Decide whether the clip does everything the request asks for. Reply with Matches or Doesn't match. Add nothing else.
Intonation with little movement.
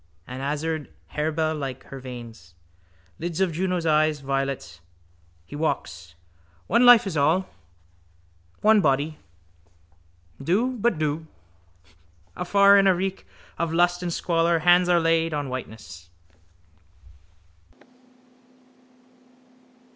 Doesn't match